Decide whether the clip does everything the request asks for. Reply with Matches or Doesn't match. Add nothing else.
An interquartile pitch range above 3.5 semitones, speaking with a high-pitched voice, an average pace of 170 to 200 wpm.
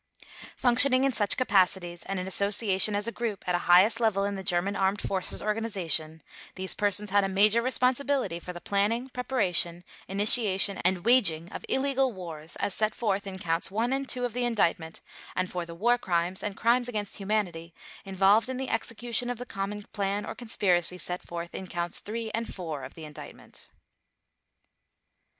Matches